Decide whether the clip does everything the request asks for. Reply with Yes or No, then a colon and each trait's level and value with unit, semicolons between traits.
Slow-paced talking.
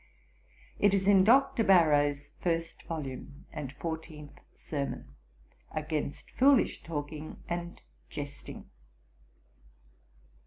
Yes: slow, 85 wpm